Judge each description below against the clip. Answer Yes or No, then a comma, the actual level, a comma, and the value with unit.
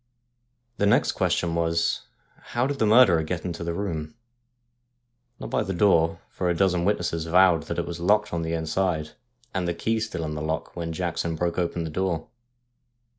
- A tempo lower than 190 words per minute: Yes, average, 180 wpm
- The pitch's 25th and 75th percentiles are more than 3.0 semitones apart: No, narrow, 2.6 semitones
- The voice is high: No, very low, 85 Hz